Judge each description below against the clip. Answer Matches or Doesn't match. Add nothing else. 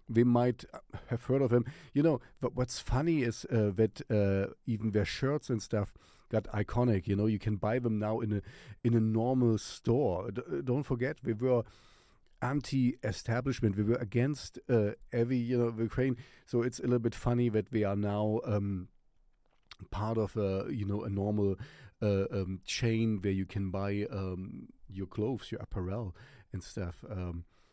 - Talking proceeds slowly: Doesn't match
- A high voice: Doesn't match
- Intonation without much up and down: Doesn't match